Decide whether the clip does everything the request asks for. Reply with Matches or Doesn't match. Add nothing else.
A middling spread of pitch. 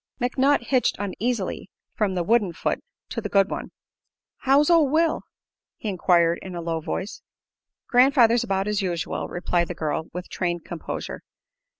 Doesn't match